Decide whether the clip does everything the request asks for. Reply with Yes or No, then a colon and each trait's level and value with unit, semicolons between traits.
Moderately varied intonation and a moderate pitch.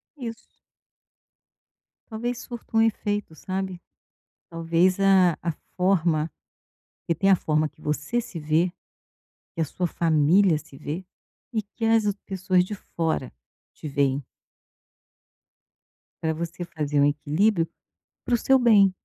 Yes: average, 4.5 semitones; medium, 175 Hz